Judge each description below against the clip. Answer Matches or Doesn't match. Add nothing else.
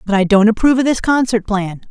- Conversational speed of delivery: Doesn't match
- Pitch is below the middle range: Doesn't match